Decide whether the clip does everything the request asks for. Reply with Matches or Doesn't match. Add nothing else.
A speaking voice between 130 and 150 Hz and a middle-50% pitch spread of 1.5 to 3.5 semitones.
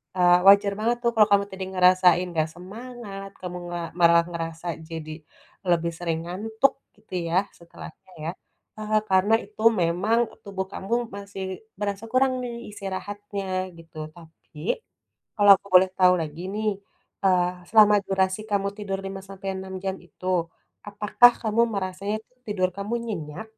Doesn't match